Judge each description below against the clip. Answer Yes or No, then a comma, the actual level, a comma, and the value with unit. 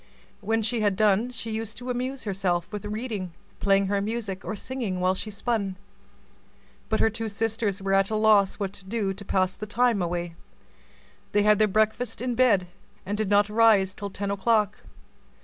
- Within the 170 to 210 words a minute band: Yes, average, 185 wpm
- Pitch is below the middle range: No, high, 210 Hz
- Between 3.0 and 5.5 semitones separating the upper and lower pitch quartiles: No, narrow, 2.5 semitones